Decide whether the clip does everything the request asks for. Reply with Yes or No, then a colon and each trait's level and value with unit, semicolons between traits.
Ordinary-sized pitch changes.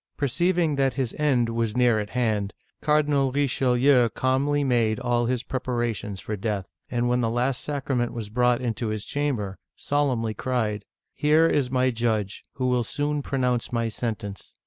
Yes: average, 3.2 semitones